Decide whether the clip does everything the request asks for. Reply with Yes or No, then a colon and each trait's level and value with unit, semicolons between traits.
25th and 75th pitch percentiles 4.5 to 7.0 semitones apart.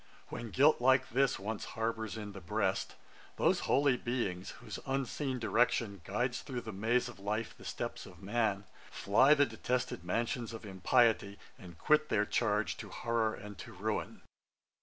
No: average, 3.5 semitones